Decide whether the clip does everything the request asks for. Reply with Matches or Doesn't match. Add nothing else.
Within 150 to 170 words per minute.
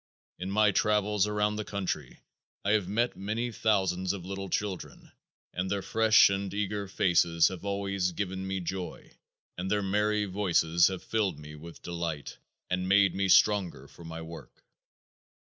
Matches